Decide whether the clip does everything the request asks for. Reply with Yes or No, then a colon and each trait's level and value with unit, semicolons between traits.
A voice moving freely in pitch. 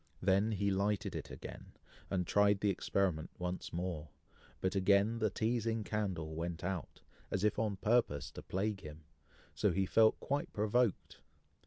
No: average, 3.0 semitones